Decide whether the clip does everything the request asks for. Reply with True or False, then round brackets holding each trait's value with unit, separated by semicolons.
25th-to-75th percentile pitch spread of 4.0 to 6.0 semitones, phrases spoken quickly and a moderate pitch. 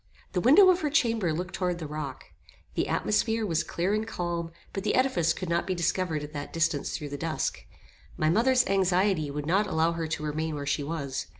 True (4.4 semitones; 210 wpm; 170 Hz)